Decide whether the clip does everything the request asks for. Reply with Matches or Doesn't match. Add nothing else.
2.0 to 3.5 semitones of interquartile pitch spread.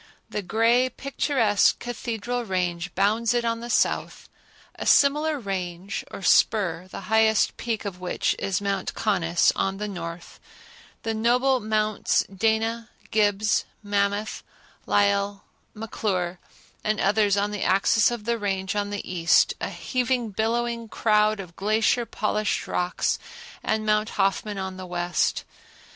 Matches